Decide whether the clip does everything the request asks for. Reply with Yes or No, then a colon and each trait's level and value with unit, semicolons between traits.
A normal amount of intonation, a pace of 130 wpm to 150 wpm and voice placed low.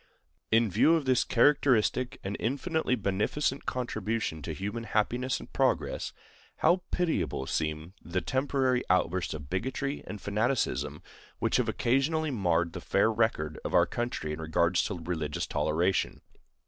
No: wide, 7.1 semitones; average, 140 wpm; low, 105 Hz